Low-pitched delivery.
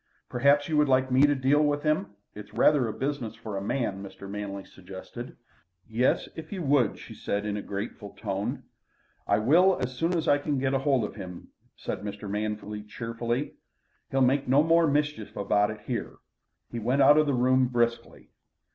Yes: low, 125 Hz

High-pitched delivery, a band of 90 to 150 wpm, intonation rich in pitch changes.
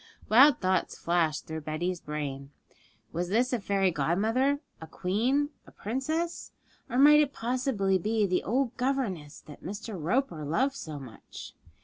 Yes: high, 200 Hz; average, 145 wpm; wide, 7.7 semitones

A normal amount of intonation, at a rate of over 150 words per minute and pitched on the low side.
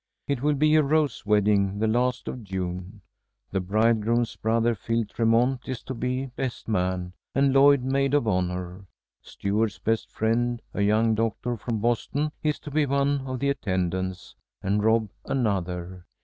Yes: average, 4.7 semitones; average, 160 wpm; low, 115 Hz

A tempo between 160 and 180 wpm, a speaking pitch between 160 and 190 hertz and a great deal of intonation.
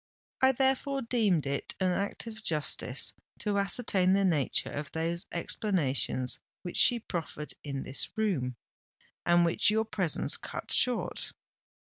No: slow, 135 wpm; medium, 185 Hz; wide, 6.3 semitones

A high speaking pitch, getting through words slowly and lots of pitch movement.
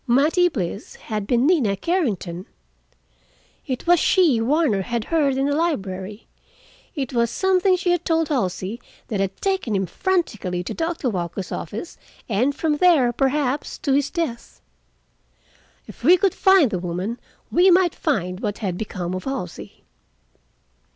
No: very high, 255 Hz; average, 150 wpm; wide, 8.8 semitones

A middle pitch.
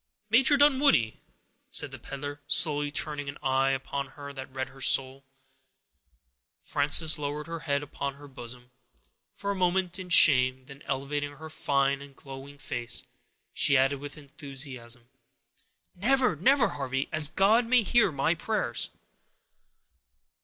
Yes: medium, 145 Hz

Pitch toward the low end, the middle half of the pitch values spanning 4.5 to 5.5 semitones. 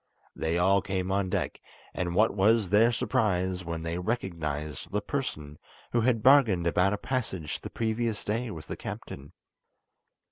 Yes: very low, 95 Hz; average, 4.8 semitones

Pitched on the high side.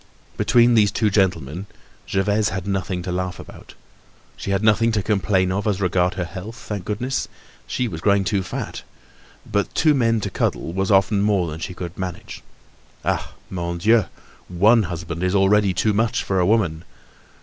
No: very low, 95 Hz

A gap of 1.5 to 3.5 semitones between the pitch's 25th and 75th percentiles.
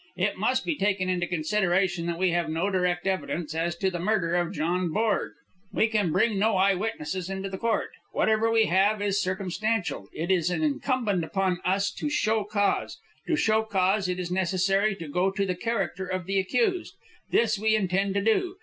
Yes: average, 3.2 semitones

